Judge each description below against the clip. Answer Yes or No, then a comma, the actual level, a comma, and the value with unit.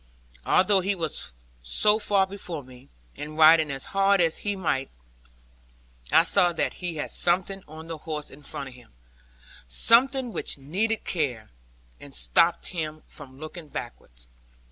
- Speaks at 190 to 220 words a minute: No, average, 155 wpm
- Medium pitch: Yes, medium, 160 Hz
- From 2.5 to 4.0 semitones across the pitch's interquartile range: No, average, 5.2 semitones